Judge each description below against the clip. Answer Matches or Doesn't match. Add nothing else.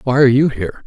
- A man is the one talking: Matches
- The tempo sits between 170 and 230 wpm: Doesn't match